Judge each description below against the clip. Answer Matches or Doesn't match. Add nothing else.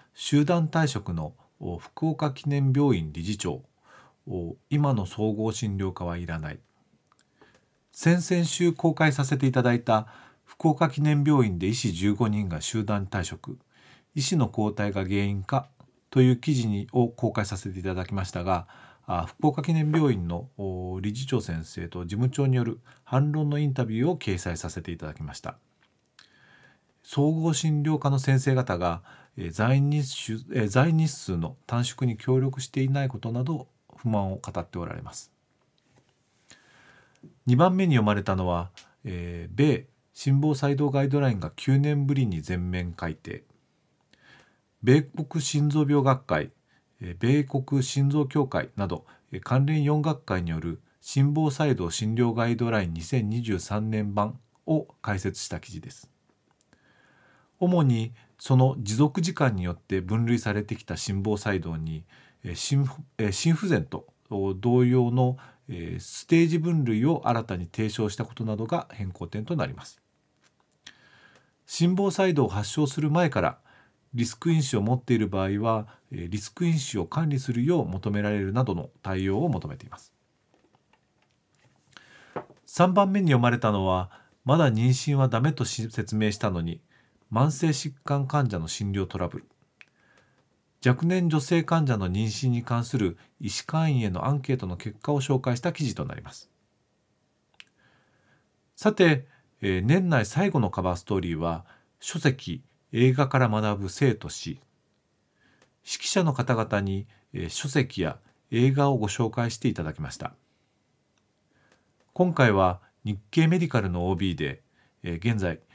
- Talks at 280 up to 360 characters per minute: Doesn't match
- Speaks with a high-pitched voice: Doesn't match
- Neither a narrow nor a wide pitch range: Doesn't match